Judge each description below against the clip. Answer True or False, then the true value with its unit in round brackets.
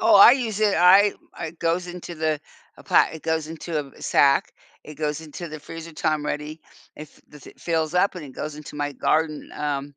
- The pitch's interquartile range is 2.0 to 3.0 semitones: True (2.5 semitones)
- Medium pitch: True (160 Hz)